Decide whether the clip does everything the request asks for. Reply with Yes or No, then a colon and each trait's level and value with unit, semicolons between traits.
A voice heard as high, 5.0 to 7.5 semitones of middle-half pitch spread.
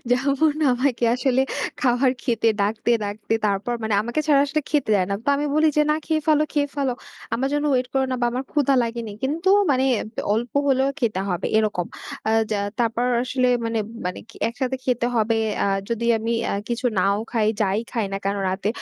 No: high, 245 Hz; average, 3.8 semitones